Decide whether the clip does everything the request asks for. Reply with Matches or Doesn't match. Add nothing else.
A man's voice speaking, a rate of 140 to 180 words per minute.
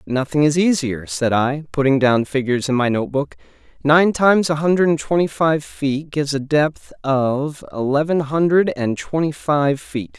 Matches